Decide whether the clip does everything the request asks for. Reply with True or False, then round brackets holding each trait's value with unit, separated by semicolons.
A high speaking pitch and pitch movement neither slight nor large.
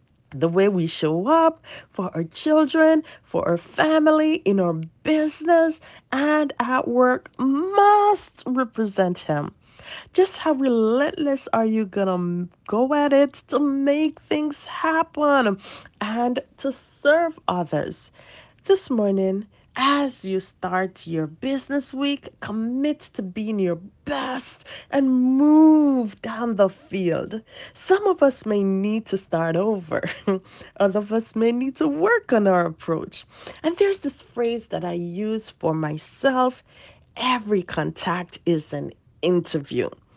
False (240 Hz; 7.4 semitones)